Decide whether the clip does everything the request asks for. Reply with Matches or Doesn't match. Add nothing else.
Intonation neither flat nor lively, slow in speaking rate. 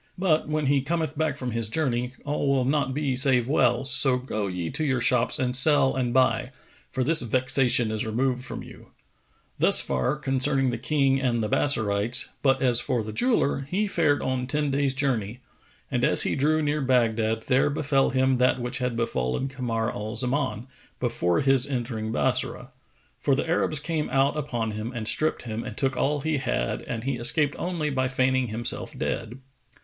Doesn't match